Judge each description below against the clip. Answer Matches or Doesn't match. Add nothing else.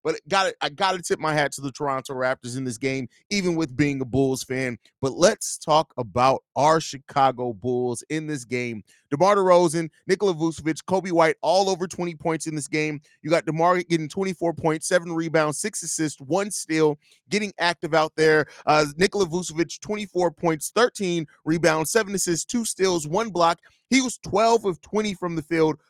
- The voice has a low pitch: Doesn't match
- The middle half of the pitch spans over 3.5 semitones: Matches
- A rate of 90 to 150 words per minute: Doesn't match